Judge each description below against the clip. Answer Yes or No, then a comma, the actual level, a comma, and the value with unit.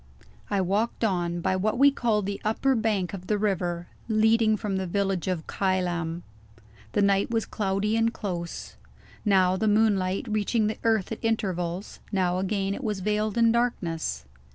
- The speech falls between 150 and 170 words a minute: Yes, average, 165 wpm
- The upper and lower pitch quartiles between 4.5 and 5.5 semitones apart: No, average, 2.9 semitones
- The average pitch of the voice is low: No, high, 200 Hz